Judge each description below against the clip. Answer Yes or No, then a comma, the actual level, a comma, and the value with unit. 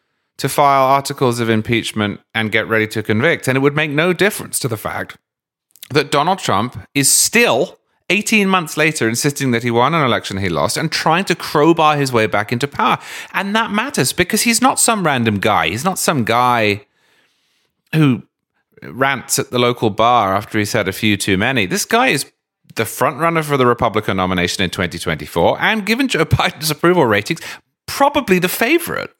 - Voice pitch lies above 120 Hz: Yes, low, 135 Hz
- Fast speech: No, average, 185 wpm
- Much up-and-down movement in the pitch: Yes, wide, 7.6 semitones